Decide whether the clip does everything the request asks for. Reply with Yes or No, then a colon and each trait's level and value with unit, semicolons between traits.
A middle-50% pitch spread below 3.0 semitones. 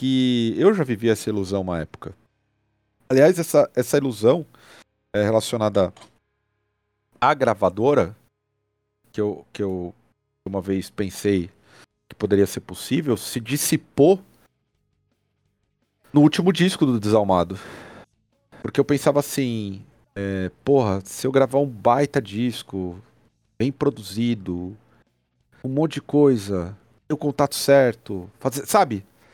No: average, 4.8 semitones